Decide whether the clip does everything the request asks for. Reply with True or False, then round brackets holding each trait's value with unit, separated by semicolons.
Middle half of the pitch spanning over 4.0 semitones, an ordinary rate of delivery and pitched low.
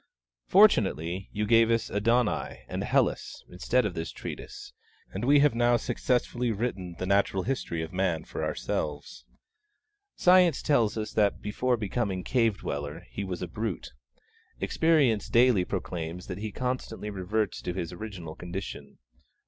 True (5.1 semitones; 145 wpm; 105 Hz)